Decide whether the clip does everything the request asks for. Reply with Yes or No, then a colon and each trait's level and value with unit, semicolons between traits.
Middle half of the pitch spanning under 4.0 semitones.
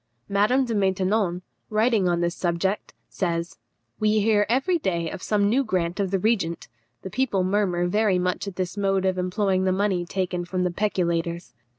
Yes: average, 2.8 semitones